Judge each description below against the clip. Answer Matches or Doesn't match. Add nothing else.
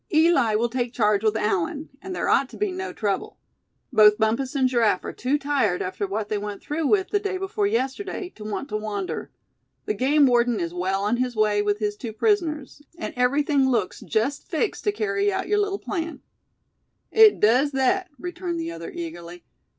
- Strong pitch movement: Matches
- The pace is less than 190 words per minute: Doesn't match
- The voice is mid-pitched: Doesn't match